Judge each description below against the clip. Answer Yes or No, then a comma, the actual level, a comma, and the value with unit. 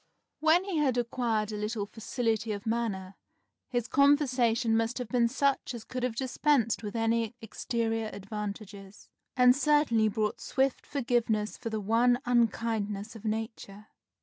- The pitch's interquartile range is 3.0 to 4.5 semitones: No, narrow, 2.5 semitones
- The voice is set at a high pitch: Yes, high, 230 Hz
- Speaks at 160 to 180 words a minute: No, average, 145 wpm